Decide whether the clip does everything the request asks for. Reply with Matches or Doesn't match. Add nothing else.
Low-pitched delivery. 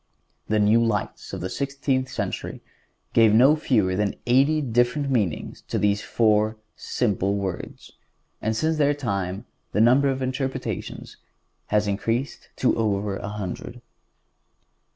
Matches